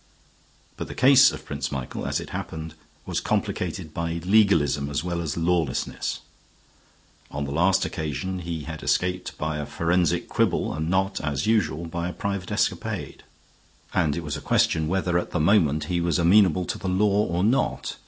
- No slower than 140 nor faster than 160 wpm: No, average, 175 wpm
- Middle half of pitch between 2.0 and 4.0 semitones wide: Yes, average, 3.3 semitones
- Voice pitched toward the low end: Yes, very low, 85 Hz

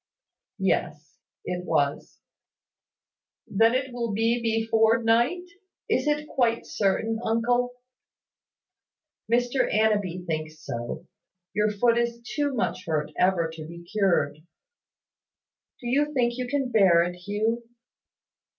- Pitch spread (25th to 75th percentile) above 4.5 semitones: Yes, average, 5.2 semitones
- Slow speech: Yes, slow, 115 wpm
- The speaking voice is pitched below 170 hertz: No, high, 225 Hz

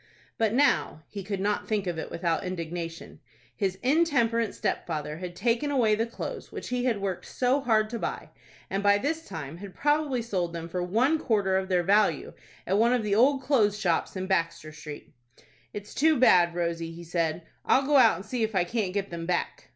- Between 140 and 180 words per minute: No, average, 195 wpm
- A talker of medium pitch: No, high, 200 Hz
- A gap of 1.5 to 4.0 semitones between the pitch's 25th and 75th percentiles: No, wide, 5.4 semitones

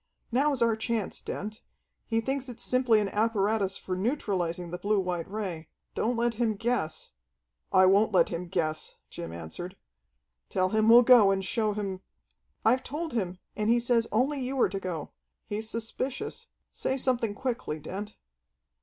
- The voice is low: No, high, 215 Hz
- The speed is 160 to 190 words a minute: Yes, average, 170 wpm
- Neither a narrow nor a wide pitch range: Yes, average, 4.5 semitones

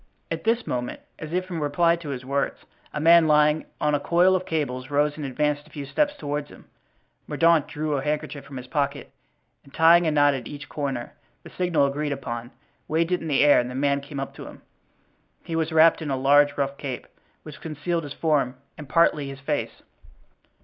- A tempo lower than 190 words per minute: No, fast, 205 wpm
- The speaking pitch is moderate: Yes, medium, 145 Hz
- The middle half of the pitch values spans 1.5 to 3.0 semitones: Yes, narrow, 2.6 semitones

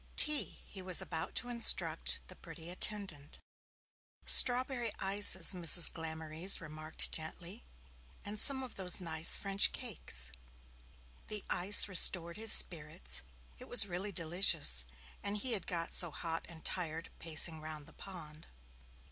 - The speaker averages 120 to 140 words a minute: Yes, slow, 135 wpm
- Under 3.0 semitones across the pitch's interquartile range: No, average, 4.2 semitones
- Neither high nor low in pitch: Yes, medium, 175 Hz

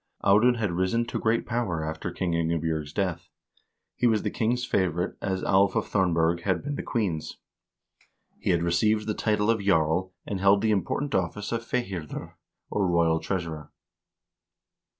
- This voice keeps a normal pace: Yes, average, 165 wpm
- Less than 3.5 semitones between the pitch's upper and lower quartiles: No, average, 4.2 semitones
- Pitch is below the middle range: Yes, very low, 95 Hz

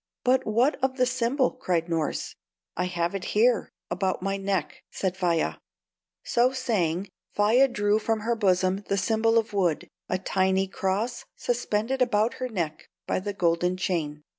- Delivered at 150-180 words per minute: Yes, average, 160 wpm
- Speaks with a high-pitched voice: Yes, high, 200 Hz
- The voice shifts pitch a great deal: No, average, 4.4 semitones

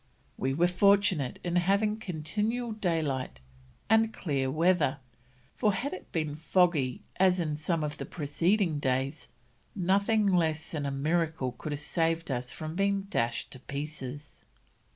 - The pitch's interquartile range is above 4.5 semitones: Yes, average, 4.9 semitones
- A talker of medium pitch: Yes, medium, 165 Hz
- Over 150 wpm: No, average, 145 wpm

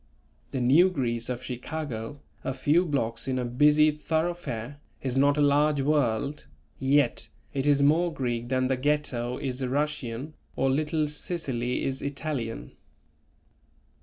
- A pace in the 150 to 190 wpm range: No, slow, 135 wpm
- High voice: No, medium, 140 Hz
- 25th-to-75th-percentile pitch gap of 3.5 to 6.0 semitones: No, average, 3.1 semitones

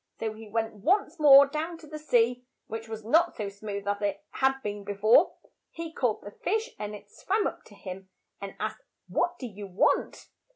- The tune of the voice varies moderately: No, wide, 6.9 semitones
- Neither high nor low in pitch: No, high, 225 Hz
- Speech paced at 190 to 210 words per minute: Yes, fast, 205 wpm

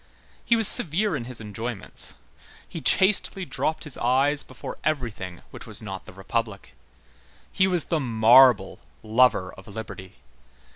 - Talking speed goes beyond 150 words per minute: No, average, 140 wpm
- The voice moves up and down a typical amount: No, wide, 6.3 semitones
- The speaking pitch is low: Yes, low, 120 Hz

